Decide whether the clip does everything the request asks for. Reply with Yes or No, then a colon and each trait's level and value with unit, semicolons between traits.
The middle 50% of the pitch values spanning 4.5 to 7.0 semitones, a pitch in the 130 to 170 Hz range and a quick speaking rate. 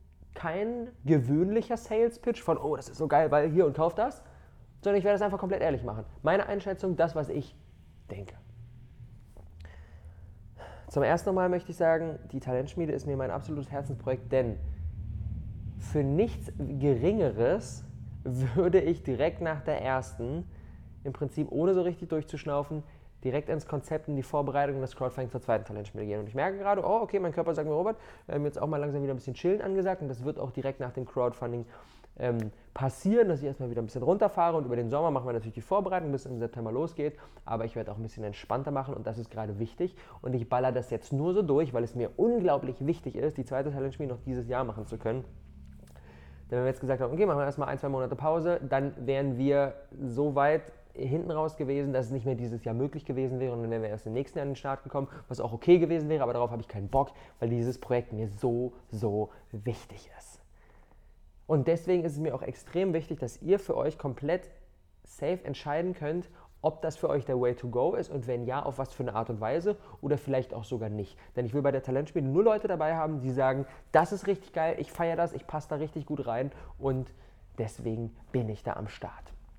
Yes: average, 5.0 semitones; low, 135 Hz; fast, 220 wpm